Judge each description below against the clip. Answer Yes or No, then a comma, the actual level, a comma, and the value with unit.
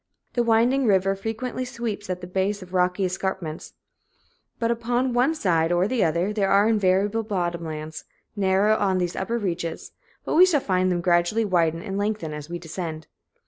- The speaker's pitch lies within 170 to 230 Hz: Yes, high, 190 Hz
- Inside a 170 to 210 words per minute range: Yes, average, 185 wpm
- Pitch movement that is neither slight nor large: Yes, average, 4.3 semitones